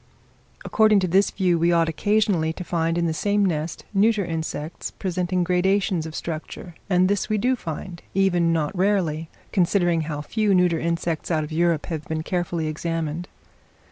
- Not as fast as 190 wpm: Yes, average, 170 wpm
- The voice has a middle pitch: Yes, medium, 175 Hz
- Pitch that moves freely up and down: No, average, 2.9 semitones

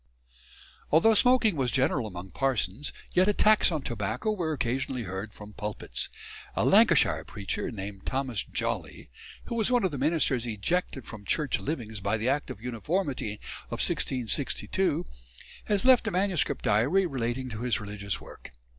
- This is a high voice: No, low, 130 Hz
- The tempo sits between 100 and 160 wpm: Yes, average, 150 wpm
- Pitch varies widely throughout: Yes, wide, 8.3 semitones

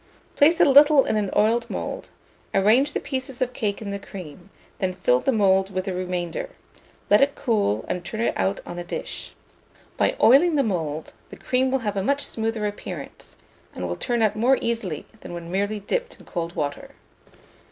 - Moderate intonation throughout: No, wide, 5.9 semitones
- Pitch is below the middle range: No, high, 210 Hz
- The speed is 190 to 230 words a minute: Yes, average, 195 wpm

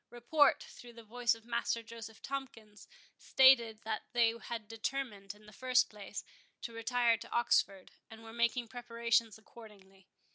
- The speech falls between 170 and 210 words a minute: No, average, 150 wpm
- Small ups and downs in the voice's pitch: Yes, narrow, 1.8 semitones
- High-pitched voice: Yes, high, 230 Hz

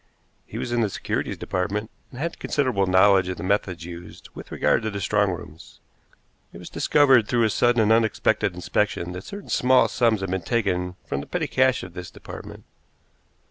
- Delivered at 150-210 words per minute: Yes, average, 190 wpm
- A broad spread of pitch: No, average, 4.7 semitones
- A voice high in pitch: No, low, 100 Hz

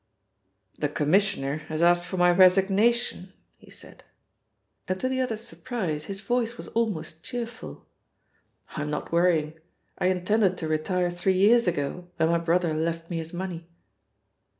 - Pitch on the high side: No, medium, 180 Hz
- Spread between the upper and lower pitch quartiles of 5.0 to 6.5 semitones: No, average, 3.9 semitones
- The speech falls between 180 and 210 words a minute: No, average, 150 wpm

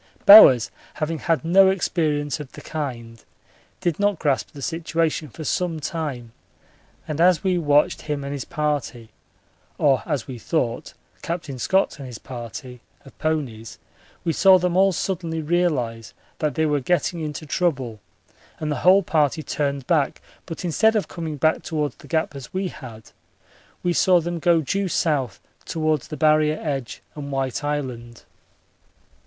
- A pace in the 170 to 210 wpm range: No, average, 160 wpm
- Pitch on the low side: No, medium, 155 Hz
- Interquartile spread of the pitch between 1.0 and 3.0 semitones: No, average, 3.9 semitones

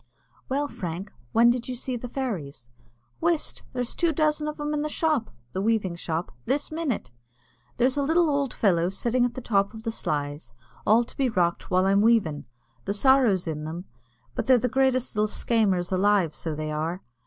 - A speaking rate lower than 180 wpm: No, average, 195 wpm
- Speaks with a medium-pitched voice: No, high, 225 Hz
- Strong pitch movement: Yes, wide, 6.7 semitones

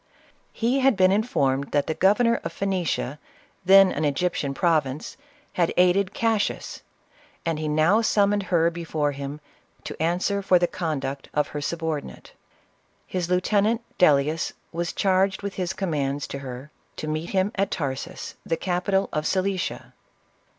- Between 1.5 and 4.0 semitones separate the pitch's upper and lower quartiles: No, average, 4.4 semitones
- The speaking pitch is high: No, medium, 175 Hz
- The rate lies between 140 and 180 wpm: Yes, average, 150 wpm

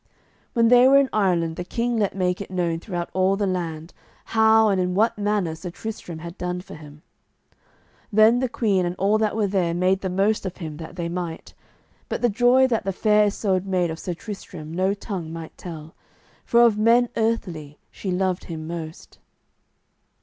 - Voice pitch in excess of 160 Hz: Yes, high, 190 Hz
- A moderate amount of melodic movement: Yes, average, 4.1 semitones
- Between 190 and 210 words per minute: Yes, average, 195 wpm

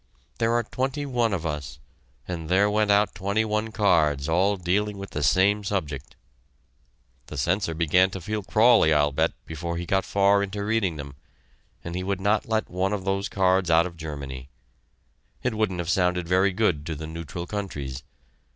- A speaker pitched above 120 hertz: No, very low, 95 Hz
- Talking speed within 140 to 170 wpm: No, average, 180 wpm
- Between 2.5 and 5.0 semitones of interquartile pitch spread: Yes, average, 4.1 semitones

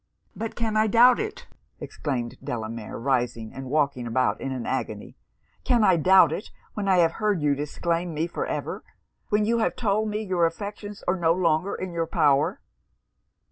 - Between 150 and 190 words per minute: Yes, average, 180 wpm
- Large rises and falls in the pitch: Yes, wide, 6.8 semitones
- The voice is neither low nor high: Yes, medium, 170 Hz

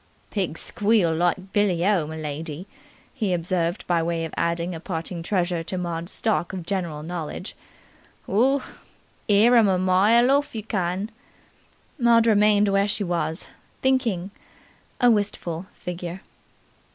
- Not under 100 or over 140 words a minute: Yes, slow, 135 wpm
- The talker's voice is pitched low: No, medium, 185 Hz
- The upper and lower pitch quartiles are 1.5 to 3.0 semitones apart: No, average, 3.7 semitones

